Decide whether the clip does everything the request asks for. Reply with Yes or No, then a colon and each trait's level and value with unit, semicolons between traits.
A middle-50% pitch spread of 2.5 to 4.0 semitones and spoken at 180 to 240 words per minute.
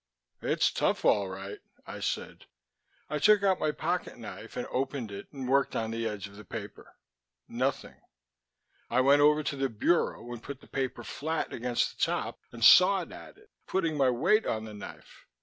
No: average, 5.3 semitones; average, 185 wpm